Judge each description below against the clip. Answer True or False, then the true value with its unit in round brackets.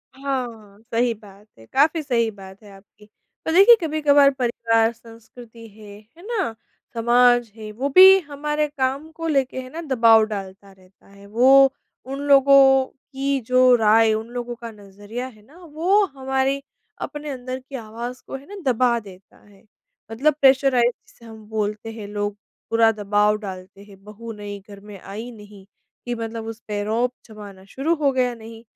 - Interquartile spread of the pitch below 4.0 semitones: False (4.3 semitones)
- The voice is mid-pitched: False (230 Hz)